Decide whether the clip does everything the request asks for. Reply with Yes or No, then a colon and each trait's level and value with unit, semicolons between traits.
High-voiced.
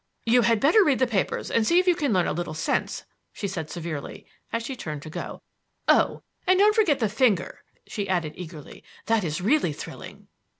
Yes: high, 215 Hz